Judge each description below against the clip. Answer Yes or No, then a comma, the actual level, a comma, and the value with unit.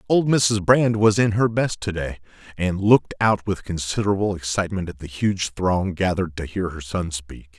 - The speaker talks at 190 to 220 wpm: Yes, average, 200 wpm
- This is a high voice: No, very low, 95 Hz